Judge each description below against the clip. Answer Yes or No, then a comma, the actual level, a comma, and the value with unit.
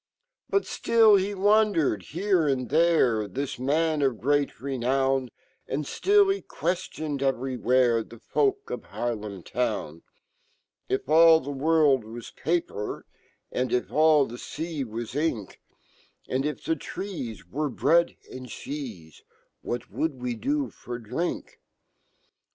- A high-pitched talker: No, medium, 140 Hz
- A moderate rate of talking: No, slow, 125 wpm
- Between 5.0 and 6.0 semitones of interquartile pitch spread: Yes, average, 5.3 semitones